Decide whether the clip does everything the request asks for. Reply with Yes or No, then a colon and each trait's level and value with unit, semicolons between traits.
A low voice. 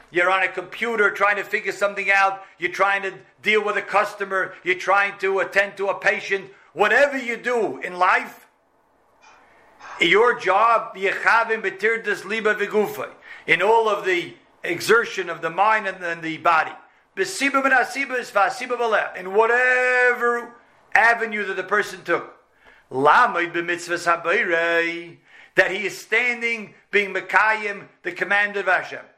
No: high, 200 Hz